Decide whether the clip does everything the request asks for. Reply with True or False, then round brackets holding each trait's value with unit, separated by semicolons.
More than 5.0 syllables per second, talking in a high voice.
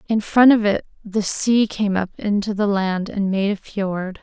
False (4.1 syllables/s; 205 Hz)